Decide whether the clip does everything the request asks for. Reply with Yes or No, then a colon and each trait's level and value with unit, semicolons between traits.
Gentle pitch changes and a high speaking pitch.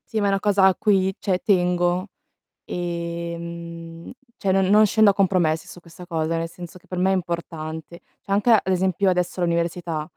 No: narrow, 2.2 semitones; medium, 180 Hz